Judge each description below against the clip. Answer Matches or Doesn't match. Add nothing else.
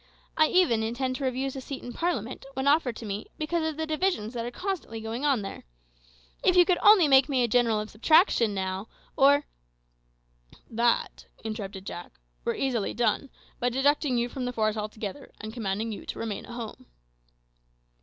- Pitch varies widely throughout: Doesn't match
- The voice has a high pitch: Matches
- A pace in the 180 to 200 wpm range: Matches